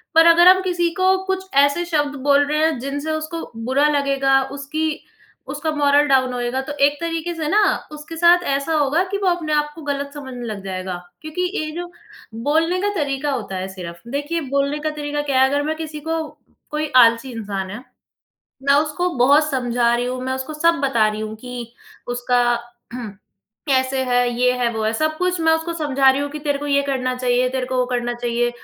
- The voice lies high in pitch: Yes, very high, 285 Hz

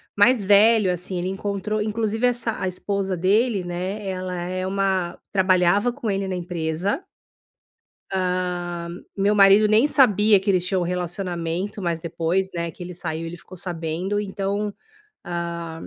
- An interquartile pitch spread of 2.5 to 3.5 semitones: Yes, average, 2.8 semitones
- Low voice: No, high, 190 Hz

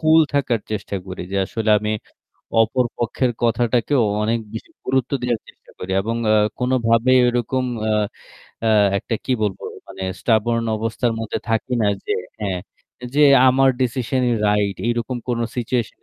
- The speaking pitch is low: Yes, low, 115 Hz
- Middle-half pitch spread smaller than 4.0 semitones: Yes, average, 2.7 semitones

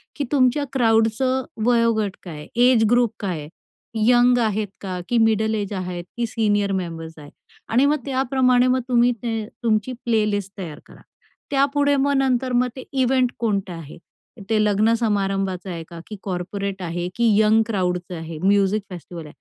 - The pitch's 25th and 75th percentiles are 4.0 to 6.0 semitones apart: Yes, average, 4.4 semitones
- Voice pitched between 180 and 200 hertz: No, high, 220 Hz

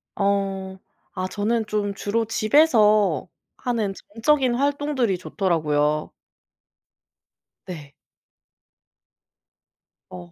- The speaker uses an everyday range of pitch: Yes, average, 4.0 semitones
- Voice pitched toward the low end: No, high, 205 Hz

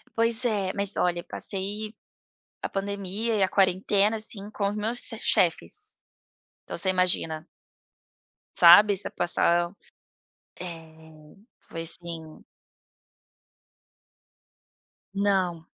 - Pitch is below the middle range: No, high, 190 Hz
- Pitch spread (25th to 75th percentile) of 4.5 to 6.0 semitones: No, average, 3.3 semitones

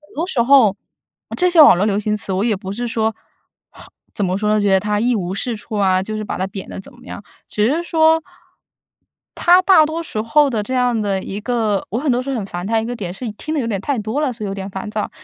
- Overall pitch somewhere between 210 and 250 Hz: Yes, high, 220 Hz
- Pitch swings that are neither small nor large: Yes, average, 4.4 semitones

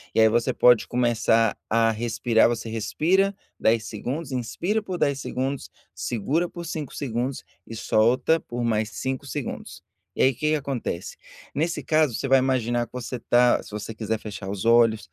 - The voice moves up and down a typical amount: Yes, average, 3.8 semitones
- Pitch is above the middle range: No, low, 120 Hz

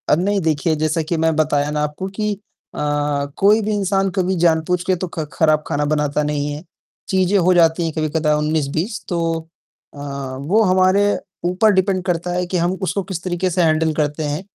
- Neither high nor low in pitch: Yes, medium, 170 Hz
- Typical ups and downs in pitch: Yes, average, 3.5 semitones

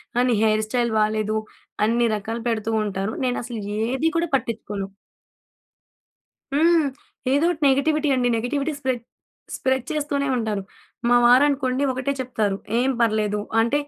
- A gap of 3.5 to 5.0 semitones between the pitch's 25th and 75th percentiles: Yes, average, 4.3 semitones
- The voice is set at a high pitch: Yes, high, 245 Hz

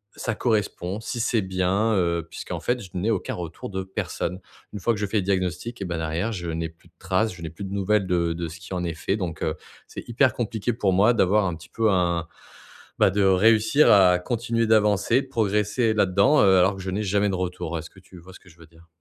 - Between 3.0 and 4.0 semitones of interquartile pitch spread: Yes, average, 3.4 semitones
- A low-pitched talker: Yes, very low, 95 Hz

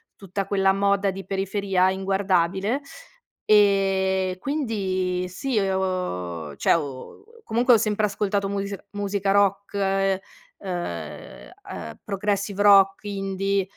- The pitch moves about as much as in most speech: No, narrow, 1.3 semitones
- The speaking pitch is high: Yes, high, 195 Hz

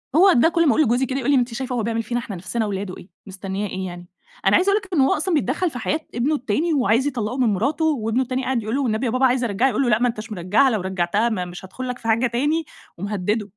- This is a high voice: Yes, high, 240 Hz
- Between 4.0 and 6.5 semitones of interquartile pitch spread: Yes, average, 4.4 semitones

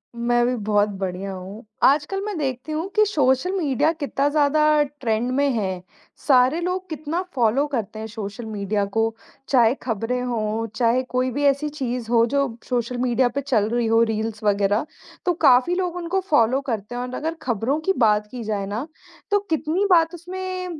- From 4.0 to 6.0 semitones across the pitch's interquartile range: Yes, average, 5.2 semitones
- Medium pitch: No, very high, 250 Hz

